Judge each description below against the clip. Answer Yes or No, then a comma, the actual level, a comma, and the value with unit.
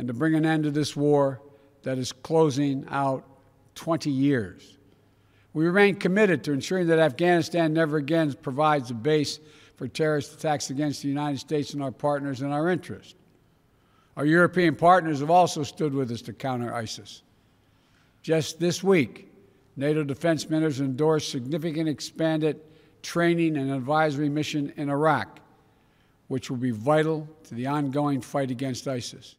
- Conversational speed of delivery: Yes, average, 155 wpm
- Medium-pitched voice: Yes, medium, 145 Hz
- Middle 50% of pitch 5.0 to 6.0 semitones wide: No, average, 2.8 semitones